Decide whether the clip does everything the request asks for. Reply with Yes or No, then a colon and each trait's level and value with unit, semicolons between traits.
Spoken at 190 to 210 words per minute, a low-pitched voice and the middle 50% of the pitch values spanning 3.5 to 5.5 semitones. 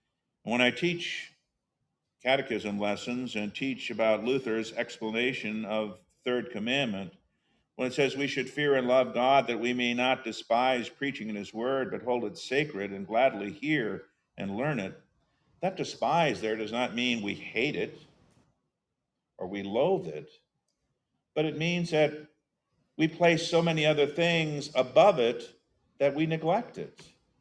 No: average, 155 wpm; low, 125 Hz; average, 4.6 semitones